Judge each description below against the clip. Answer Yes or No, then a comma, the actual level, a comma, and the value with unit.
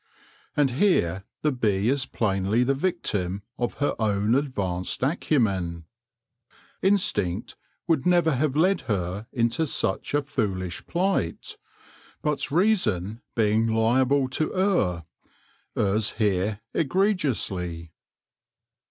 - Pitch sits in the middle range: No, low, 115 Hz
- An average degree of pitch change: No, wide, 7.4 semitones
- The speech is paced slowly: Yes, slow, 105 wpm